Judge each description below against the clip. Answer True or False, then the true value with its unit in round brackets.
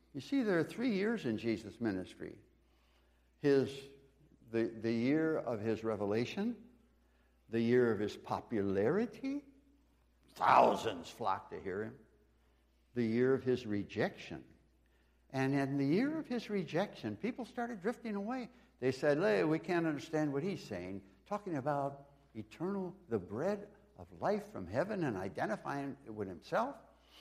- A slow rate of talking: False (145 wpm)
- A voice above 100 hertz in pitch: True (140 Hz)